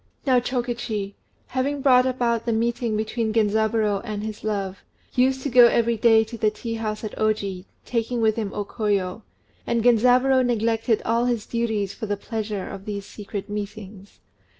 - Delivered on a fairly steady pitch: Yes, narrow, 2.3 semitones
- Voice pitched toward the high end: Yes, high, 220 Hz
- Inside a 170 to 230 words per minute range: Yes, average, 175 wpm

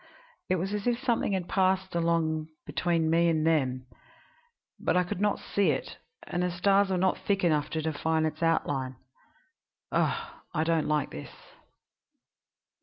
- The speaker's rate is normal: Yes, average, 160 wpm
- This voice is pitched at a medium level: Yes, medium, 170 Hz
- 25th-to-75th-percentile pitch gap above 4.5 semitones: No, average, 3.2 semitones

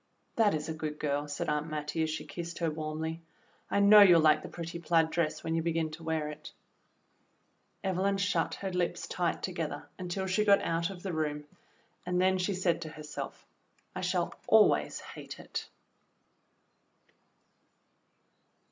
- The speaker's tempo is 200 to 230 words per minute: No, average, 165 wpm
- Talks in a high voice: No, medium, 165 Hz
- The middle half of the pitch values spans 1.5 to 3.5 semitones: Yes, average, 3.0 semitones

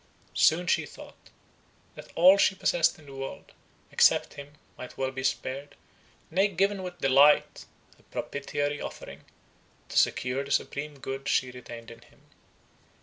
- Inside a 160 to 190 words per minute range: No, average, 145 wpm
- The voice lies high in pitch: No, medium, 140 Hz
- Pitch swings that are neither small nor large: Yes, average, 4.0 semitones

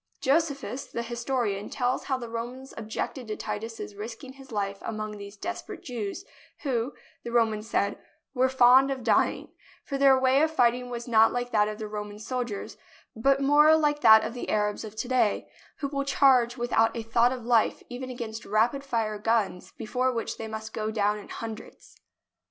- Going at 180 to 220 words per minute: Yes, average, 185 wpm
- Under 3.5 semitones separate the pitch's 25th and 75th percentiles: Yes, average, 3.1 semitones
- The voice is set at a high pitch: Yes, high, 235 Hz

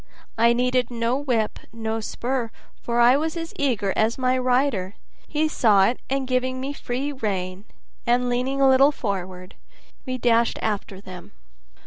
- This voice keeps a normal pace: Yes, average, 160 wpm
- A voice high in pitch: Yes, high, 245 Hz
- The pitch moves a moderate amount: Yes, average, 3.2 semitones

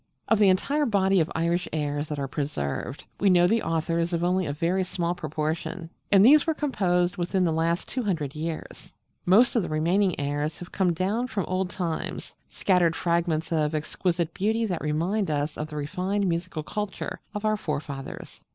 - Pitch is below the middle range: No, medium, 175 Hz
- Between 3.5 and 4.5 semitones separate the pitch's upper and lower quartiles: Yes, average, 3.8 semitones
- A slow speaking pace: No, average, 185 wpm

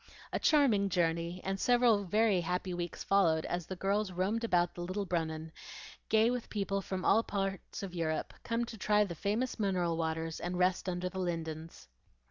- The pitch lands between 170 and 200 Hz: Yes, medium, 185 Hz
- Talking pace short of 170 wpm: No, average, 180 wpm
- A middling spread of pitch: Yes, average, 3.3 semitones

